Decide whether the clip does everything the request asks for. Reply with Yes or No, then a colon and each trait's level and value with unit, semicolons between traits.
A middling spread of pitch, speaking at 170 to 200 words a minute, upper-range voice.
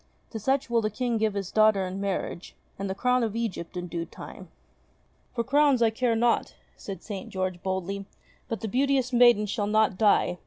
Yes: average, 3.7 semitones; average, 195 wpm; high, 215 Hz